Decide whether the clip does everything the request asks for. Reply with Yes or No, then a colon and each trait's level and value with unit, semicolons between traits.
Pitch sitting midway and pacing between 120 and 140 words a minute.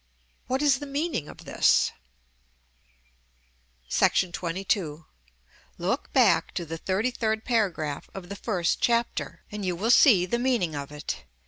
No: high, 195 Hz; slow, 135 wpm